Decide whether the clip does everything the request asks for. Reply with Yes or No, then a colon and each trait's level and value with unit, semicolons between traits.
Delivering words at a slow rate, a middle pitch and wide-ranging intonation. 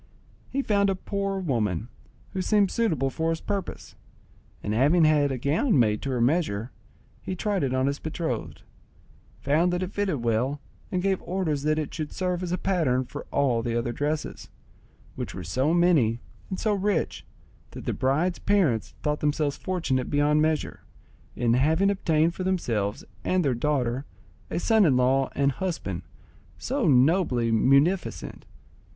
No: average, 165 wpm; medium, 150 Hz; wide, 6.1 semitones